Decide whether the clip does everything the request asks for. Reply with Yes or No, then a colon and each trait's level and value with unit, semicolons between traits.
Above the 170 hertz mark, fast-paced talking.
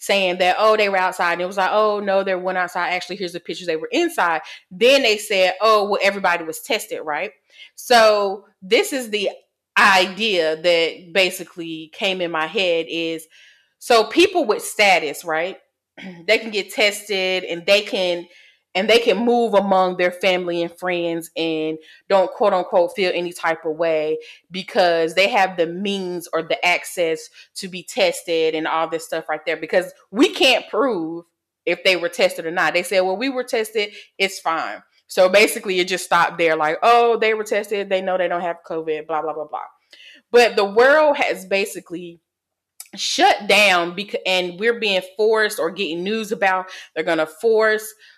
No: medium, 185 Hz; average, 185 wpm